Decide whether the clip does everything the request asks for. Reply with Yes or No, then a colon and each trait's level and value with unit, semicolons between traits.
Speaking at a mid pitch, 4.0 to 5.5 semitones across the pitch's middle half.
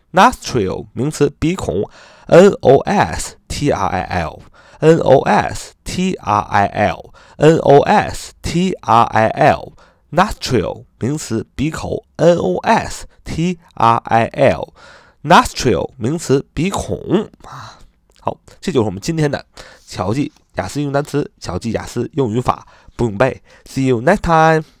Yes: medium, 145 Hz; average, 5.2 semitones